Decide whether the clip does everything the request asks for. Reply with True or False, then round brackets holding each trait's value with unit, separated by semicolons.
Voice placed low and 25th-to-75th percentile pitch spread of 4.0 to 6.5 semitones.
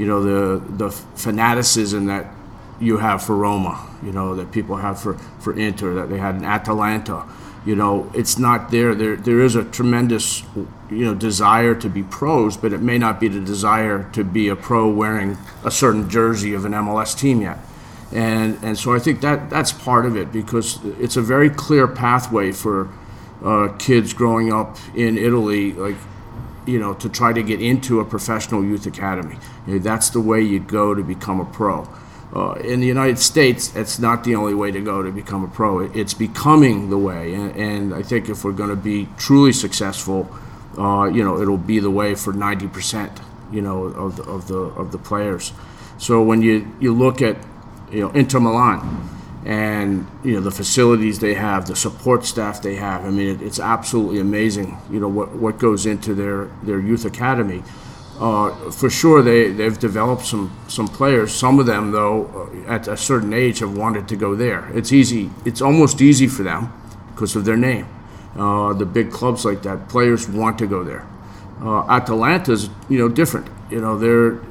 False (110 Hz; 2.6 semitones)